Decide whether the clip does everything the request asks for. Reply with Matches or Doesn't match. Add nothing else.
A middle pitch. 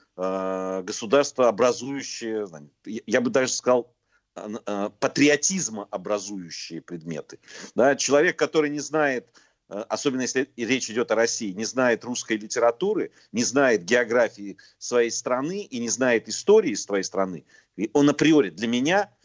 Doesn't match